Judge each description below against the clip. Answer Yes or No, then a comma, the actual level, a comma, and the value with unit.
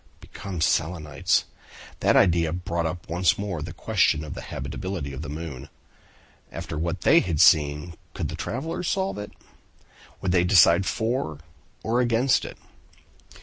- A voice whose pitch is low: Yes, very low, 85 Hz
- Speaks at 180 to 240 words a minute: No, average, 145 wpm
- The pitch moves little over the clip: No, average, 4.3 semitones